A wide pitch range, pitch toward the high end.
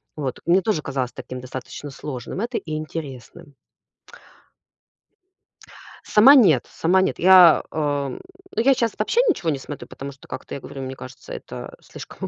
No: wide, 5.8 semitones; medium, 155 Hz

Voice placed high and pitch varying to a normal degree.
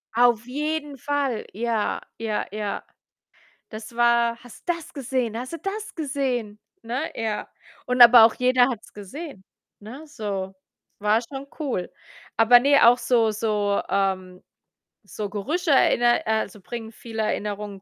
Yes: high, 235 Hz; average, 3.9 semitones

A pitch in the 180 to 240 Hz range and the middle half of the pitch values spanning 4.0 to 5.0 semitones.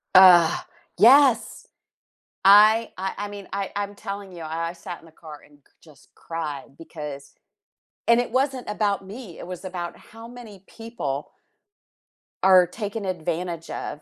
Yes: high, 190 Hz; average, 4.3 semitones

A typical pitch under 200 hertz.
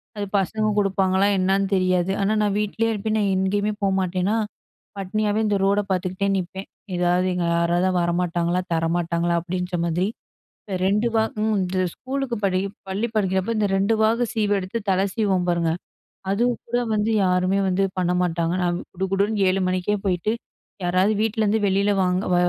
Yes: high, 190 Hz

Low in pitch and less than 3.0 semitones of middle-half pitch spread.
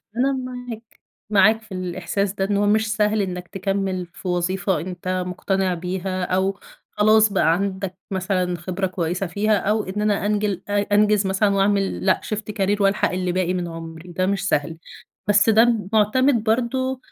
No: high, 195 Hz; narrow, 2.5 semitones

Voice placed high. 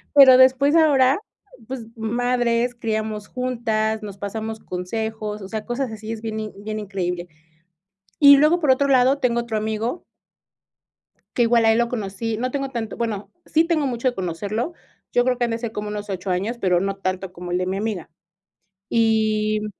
Yes: high, 225 Hz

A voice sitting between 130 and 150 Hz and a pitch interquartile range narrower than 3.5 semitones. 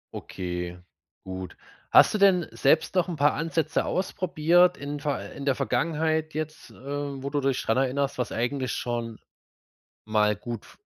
No: medium, 140 Hz; average, 4.8 semitones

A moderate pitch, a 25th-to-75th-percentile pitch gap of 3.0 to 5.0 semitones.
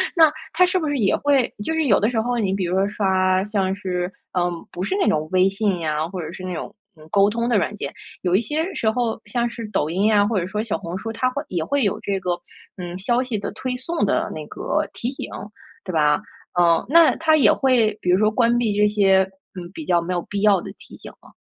No: high, 205 Hz; average, 4.7 semitones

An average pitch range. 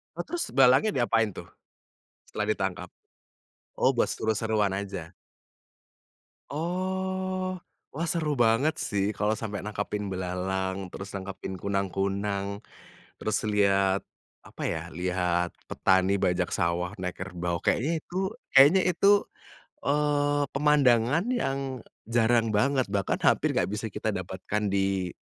No: wide, 7.0 semitones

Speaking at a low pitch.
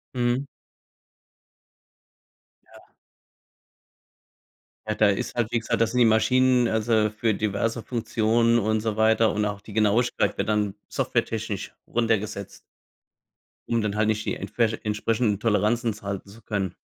Yes: low, 110 Hz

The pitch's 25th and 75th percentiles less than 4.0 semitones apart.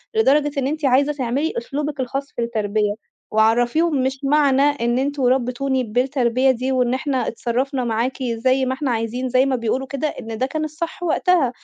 Yes: average, 2.8 semitones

